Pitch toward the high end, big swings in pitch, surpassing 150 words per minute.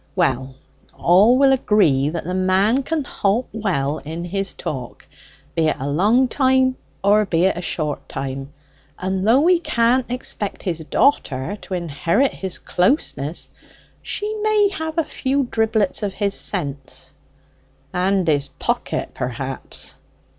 No: high, 195 Hz; wide, 8.1 semitones; average, 140 wpm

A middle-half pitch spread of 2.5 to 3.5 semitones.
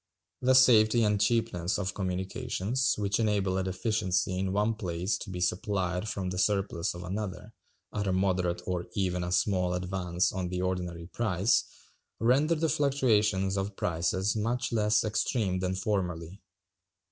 Yes: average, 2.9 semitones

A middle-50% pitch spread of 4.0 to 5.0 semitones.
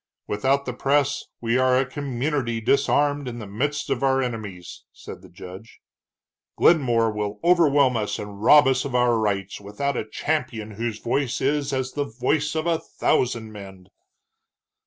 Yes: average, 4.5 semitones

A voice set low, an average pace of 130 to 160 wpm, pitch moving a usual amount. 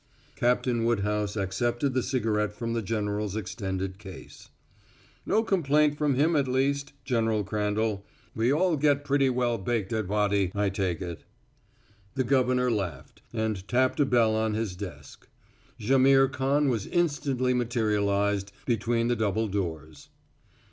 Yes: low, 115 Hz; average, 140 wpm; average, 4.3 semitones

